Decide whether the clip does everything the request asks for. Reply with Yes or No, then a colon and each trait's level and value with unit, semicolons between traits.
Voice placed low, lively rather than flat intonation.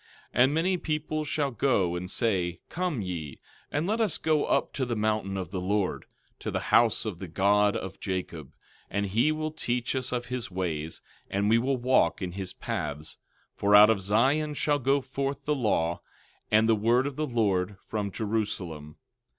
Yes: low, 110 Hz; wide, 6.4 semitones